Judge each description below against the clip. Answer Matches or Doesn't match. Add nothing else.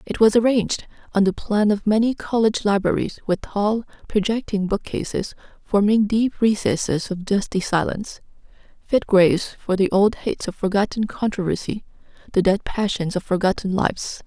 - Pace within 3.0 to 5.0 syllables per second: Doesn't match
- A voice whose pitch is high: Matches